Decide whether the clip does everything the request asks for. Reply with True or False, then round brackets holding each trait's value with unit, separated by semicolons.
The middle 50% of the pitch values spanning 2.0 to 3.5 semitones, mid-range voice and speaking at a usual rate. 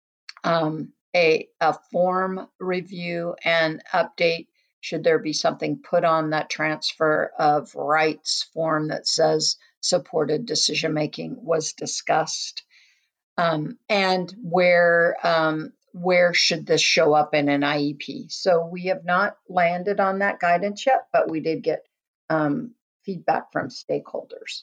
False (3.1 semitones; 170 Hz; 130 wpm)